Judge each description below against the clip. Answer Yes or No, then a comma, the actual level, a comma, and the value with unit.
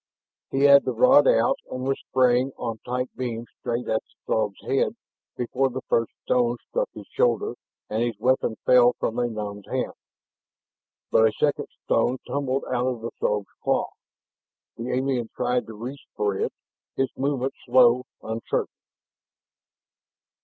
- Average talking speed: Yes, average, 155 wpm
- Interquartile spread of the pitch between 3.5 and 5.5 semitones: No, narrow, 2.4 semitones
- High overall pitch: No, low, 125 Hz